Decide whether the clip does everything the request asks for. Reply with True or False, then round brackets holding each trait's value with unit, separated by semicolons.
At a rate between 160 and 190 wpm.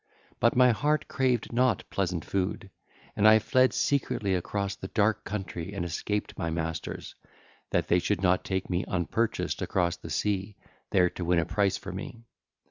True (170 wpm)